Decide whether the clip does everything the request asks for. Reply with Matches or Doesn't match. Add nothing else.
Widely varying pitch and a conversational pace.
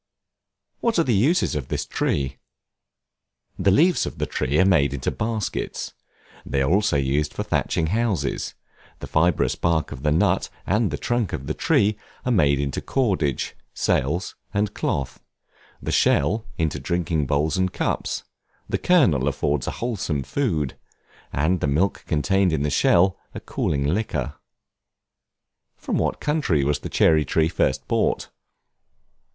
Matches